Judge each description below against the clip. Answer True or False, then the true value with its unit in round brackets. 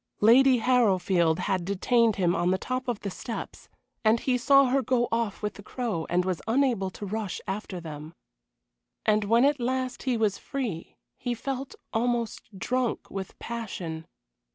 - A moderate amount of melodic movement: True (4.7 semitones)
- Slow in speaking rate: False (165 wpm)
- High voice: True (220 Hz)